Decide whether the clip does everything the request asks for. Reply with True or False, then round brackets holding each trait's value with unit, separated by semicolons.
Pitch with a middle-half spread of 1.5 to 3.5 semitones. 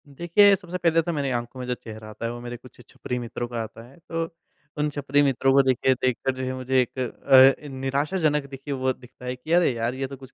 True (3.0 semitones)